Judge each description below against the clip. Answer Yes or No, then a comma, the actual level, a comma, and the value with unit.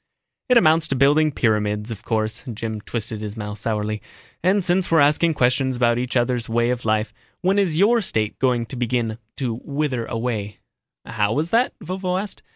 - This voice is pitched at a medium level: No, low, 125 Hz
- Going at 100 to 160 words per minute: No, average, 180 wpm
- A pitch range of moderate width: No, wide, 6.0 semitones